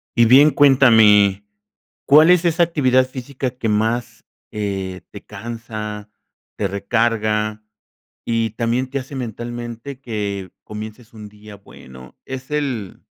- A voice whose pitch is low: Yes, low, 115 Hz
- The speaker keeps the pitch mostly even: No, average, 3.6 semitones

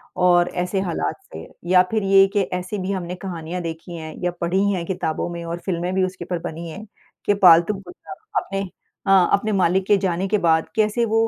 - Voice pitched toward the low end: No, medium, 180 Hz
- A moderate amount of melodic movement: No, narrow, 2.3 semitones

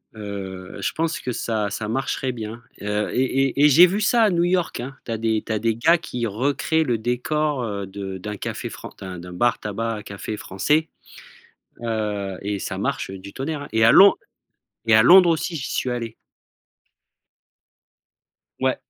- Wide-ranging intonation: Yes, wide, 5.8 semitones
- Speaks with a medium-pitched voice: No, low, 115 Hz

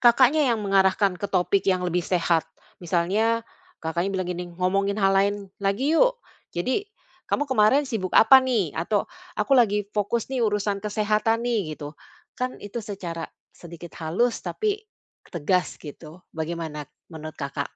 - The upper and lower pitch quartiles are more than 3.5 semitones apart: Yes, average, 4.9 semitones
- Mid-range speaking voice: No, high, 200 Hz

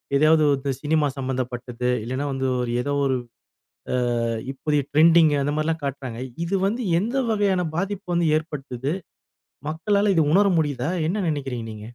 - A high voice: No, medium, 150 Hz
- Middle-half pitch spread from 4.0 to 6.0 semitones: Yes, average, 4.5 semitones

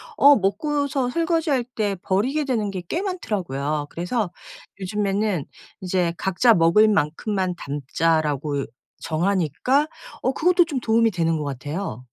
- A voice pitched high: Yes, high, 200 Hz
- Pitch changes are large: Yes, wide, 7.6 semitones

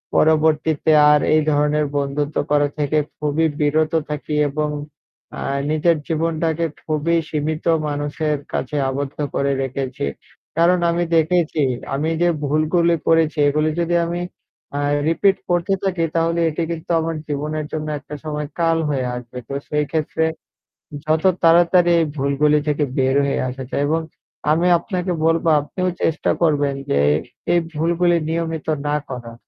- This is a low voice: No, medium, 155 Hz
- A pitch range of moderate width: No, narrow, 2.1 semitones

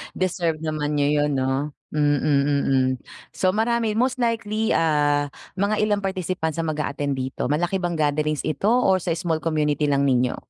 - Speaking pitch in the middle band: Yes, medium, 155 Hz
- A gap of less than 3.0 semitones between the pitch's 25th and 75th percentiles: No, average, 4.6 semitones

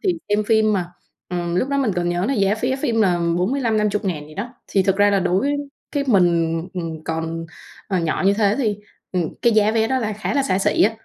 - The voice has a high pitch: Yes, high, 200 Hz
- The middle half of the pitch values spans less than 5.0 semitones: Yes, average, 4.2 semitones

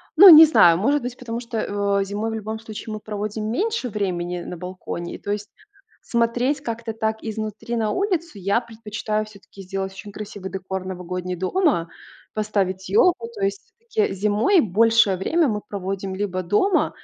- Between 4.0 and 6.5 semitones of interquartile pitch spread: No, average, 3.5 semitones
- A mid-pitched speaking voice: No, high, 215 Hz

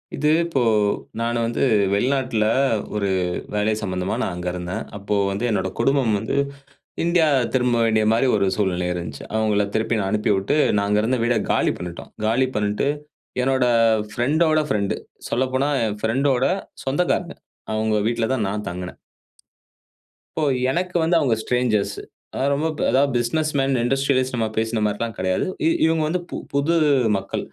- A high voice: No, low, 115 Hz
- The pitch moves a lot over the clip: No, average, 4.6 semitones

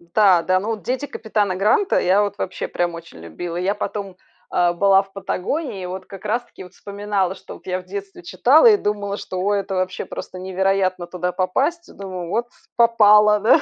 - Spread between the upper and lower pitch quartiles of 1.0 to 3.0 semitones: Yes, narrow, 2.4 semitones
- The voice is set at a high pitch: Yes, high, 195 Hz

